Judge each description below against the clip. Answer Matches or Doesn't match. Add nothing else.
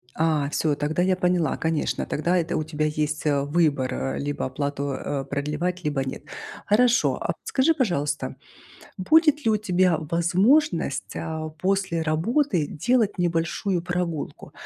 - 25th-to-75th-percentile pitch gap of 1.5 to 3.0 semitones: Doesn't match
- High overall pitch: Doesn't match